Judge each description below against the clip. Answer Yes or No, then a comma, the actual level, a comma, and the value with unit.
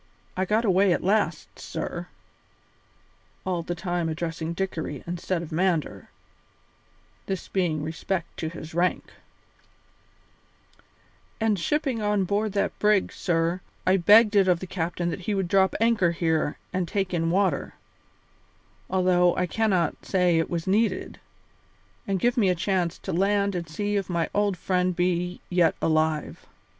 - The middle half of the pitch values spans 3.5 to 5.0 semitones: No, average, 2.8 semitones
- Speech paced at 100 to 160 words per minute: Yes, average, 150 wpm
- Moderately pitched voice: Yes, medium, 180 Hz